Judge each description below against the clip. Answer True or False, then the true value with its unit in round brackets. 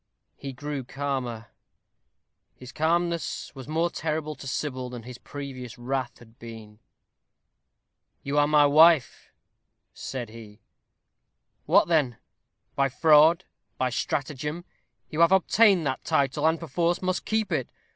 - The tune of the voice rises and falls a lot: False (4.1 semitones)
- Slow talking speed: True (125 wpm)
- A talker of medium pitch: True (145 Hz)